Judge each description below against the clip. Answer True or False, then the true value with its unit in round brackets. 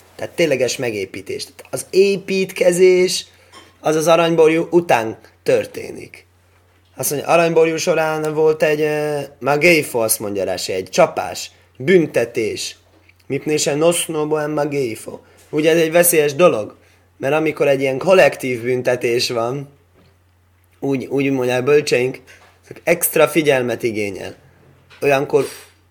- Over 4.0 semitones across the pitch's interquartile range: True (5.1 semitones)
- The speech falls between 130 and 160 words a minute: False (115 wpm)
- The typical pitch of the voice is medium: True (150 Hz)